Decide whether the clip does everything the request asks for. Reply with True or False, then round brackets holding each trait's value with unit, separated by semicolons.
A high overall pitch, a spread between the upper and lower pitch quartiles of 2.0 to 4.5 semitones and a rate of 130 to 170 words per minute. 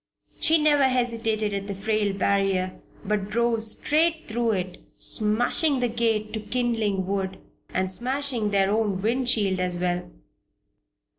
True (215 Hz; 3.6 semitones; 140 wpm)